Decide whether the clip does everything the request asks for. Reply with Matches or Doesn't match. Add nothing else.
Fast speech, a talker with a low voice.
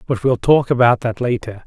Matches